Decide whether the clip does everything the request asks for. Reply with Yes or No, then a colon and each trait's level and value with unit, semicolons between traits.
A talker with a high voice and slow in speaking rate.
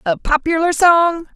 Yes: very high, 320 Hz; slow, 130 wpm